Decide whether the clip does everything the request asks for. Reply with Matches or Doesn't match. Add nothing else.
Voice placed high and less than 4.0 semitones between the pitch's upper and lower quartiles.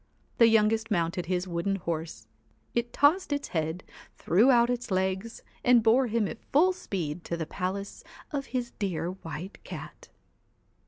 Doesn't match